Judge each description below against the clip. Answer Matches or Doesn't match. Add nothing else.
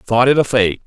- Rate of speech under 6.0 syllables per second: Matches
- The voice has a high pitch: Doesn't match